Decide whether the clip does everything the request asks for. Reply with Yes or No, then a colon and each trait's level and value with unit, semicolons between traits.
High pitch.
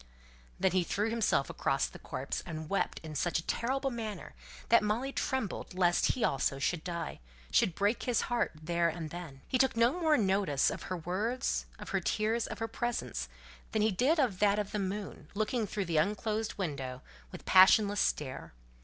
Yes: high, 200 Hz